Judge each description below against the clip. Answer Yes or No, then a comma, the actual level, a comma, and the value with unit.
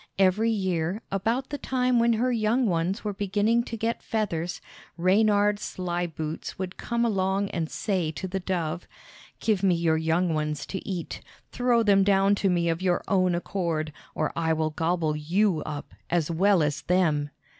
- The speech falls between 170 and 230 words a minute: Yes, average, 175 wpm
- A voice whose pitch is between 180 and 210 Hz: Yes, medium, 185 Hz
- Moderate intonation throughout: Yes, average, 3.9 semitones